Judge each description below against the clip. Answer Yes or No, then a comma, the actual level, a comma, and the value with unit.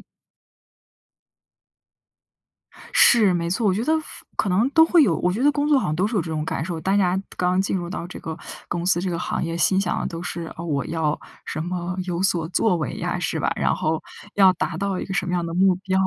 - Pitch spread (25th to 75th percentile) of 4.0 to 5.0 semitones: No, narrow, 2.5 semitones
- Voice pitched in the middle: Yes, medium, 180 Hz